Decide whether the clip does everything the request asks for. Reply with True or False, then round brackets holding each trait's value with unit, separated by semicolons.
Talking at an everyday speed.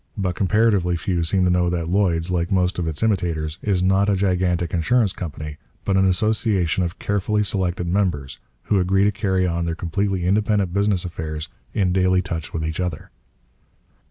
True (180 wpm)